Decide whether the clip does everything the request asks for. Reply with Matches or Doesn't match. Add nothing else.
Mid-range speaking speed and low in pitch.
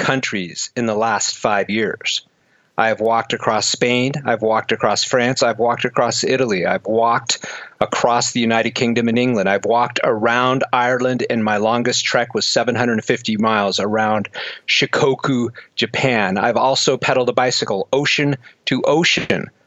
Matches